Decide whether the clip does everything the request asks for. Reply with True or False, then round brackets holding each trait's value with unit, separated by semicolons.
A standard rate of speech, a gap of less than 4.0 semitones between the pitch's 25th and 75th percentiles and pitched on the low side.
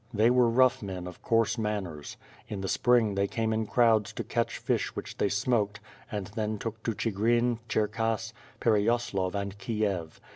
True (175 wpm; 2.4 semitones; 110 Hz)